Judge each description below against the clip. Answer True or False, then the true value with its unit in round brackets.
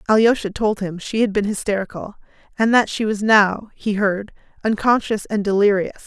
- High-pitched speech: True (210 Hz)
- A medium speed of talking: True (170 wpm)